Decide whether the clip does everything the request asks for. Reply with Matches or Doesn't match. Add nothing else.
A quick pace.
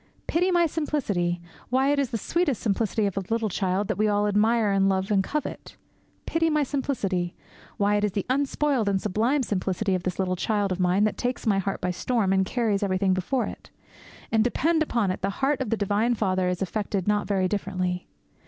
Matches